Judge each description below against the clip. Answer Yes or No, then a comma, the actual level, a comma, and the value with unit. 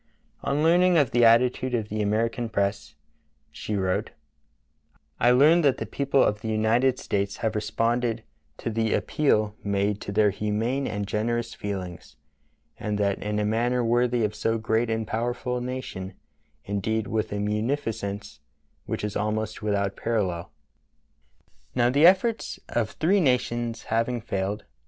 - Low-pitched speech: Yes, low, 110 Hz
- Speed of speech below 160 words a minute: Yes, average, 150 wpm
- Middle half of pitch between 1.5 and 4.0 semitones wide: Yes, average, 2.9 semitones